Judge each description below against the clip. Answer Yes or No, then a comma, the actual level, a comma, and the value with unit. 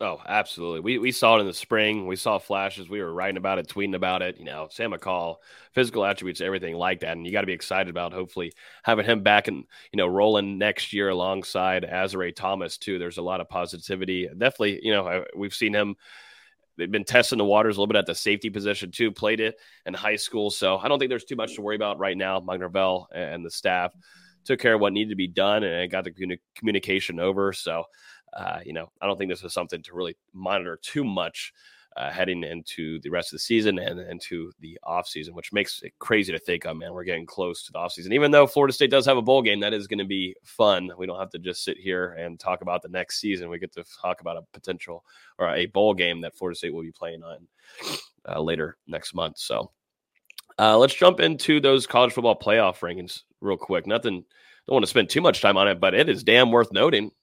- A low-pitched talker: Yes, very low, 95 Hz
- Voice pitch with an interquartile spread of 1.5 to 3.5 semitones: Yes, average, 2.8 semitones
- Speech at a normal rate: No, fast, 240 wpm